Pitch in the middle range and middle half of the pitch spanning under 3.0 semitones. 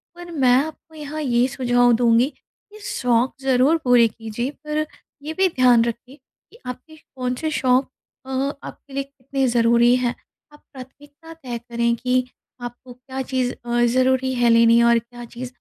No: very high, 255 Hz; narrow, 2.5 semitones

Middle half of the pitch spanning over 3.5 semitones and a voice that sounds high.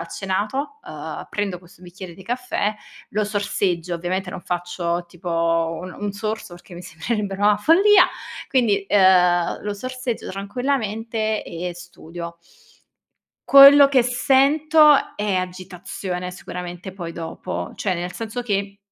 Yes: average, 4.3 semitones; high, 195 Hz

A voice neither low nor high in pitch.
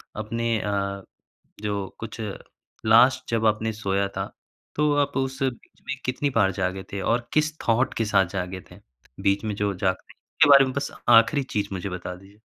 No: low, 110 Hz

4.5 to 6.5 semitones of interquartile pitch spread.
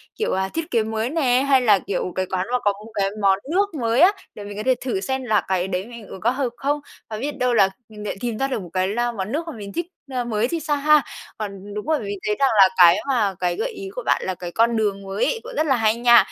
Yes: average, 5.1 semitones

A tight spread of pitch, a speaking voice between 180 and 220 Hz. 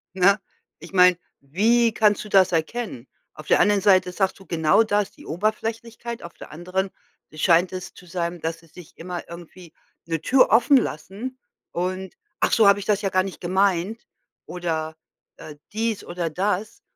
No: average, 3.5 semitones; medium, 185 Hz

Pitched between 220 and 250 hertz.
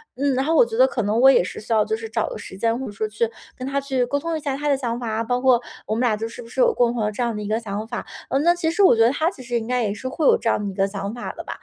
Yes: high, 235 Hz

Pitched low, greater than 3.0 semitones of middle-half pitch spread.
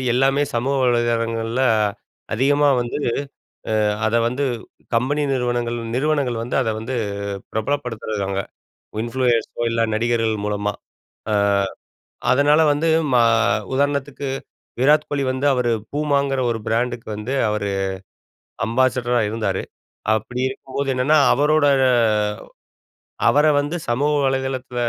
Yes: low, 125 Hz; average, 3.5 semitones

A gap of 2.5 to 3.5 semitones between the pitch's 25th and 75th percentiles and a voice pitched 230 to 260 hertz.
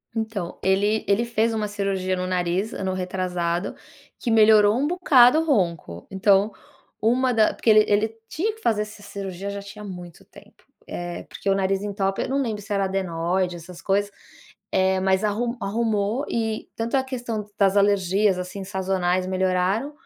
No: average, 2.9 semitones; high, 200 Hz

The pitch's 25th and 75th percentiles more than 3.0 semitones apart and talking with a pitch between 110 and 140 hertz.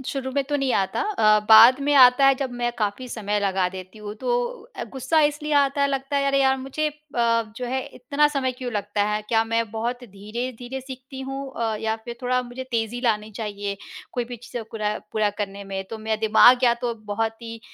No: average, 3.6 semitones; high, 240 Hz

